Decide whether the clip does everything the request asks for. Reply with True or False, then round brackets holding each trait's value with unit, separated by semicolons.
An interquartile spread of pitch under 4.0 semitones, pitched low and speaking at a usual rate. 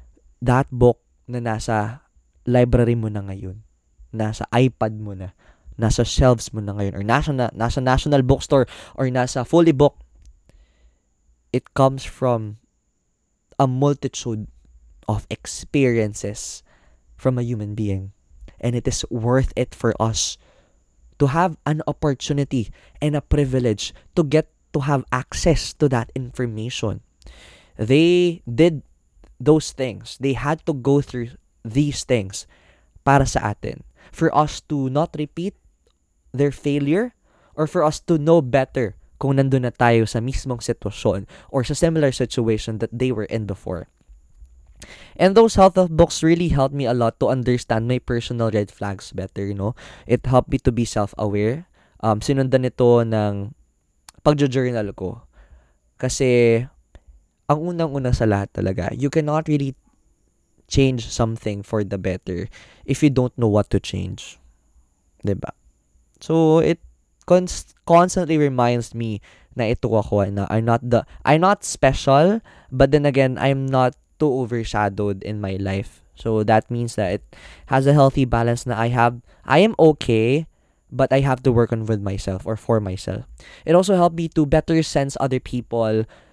False (5.1 semitones; 120 Hz; 145 wpm)